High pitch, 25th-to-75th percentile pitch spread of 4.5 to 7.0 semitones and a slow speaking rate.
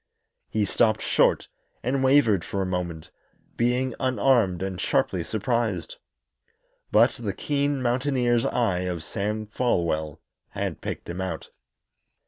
No: low, 110 Hz; wide, 5.6 semitones; slow, 120 wpm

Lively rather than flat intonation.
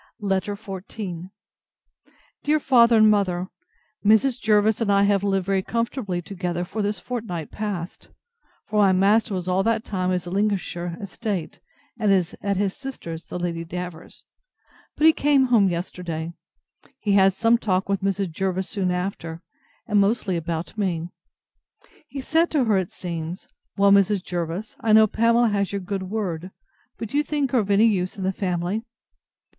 No: average, 3.3 semitones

